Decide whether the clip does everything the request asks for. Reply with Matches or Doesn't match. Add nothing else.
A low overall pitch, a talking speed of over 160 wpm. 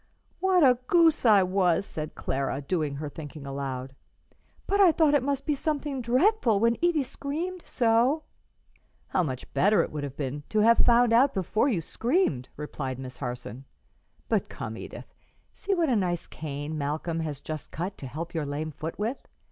Doesn't match